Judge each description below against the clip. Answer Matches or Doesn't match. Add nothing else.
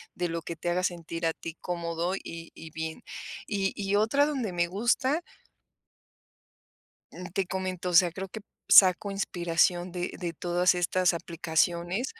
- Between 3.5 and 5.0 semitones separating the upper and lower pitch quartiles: Doesn't match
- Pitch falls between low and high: Matches